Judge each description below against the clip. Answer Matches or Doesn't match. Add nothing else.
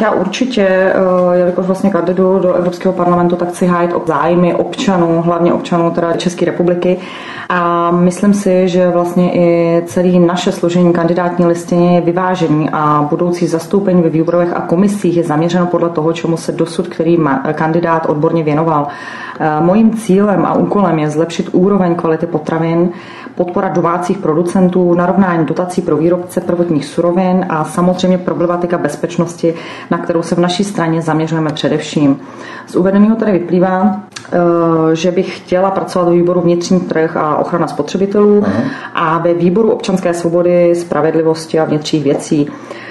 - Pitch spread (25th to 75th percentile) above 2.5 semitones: Doesn't match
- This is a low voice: Doesn't match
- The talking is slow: Doesn't match